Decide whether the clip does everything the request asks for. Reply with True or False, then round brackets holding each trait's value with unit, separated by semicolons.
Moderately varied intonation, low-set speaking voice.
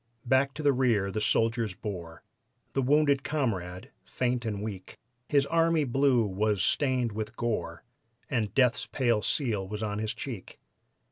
True (4.4 semitones; 115 Hz)